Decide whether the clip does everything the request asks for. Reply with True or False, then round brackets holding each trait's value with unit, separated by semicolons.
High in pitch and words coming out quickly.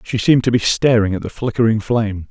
False (110 Hz; 235 wpm)